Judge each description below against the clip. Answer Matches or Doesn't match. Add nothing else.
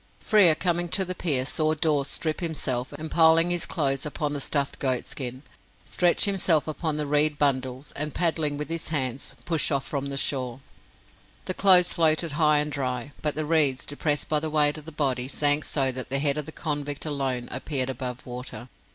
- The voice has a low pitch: Doesn't match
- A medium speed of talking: Matches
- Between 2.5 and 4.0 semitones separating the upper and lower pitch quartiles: Matches